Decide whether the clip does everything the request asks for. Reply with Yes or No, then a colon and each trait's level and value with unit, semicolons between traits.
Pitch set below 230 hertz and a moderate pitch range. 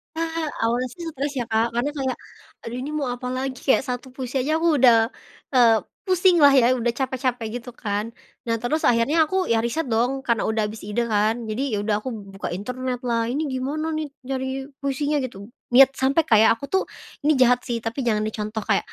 No: very high, 250 Hz; average, 3.3 semitones